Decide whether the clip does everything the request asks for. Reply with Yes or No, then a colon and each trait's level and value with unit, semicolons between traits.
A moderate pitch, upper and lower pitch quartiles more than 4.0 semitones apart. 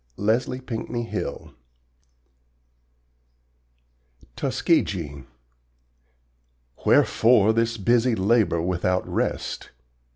No: low, 110 Hz; average, 4.4 semitones